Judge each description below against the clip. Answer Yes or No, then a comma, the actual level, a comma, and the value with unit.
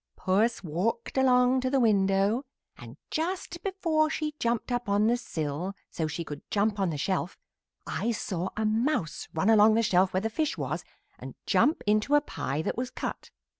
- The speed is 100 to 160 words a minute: No, average, 185 wpm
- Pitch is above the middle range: Yes, high, 220 Hz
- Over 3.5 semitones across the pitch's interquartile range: Yes, average, 5.2 semitones